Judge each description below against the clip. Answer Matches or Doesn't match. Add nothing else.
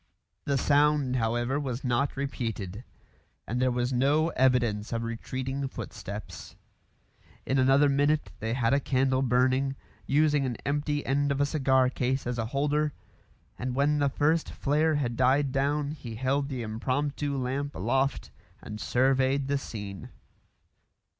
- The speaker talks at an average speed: Matches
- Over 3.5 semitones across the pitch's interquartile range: Doesn't match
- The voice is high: Doesn't match